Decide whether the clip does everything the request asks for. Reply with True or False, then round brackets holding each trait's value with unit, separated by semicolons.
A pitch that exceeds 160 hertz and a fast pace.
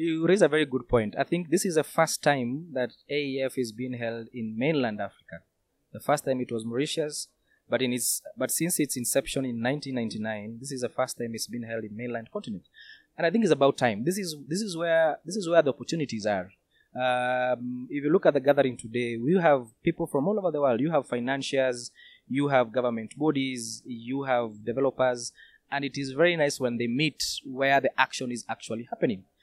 False (130 Hz; 210 wpm)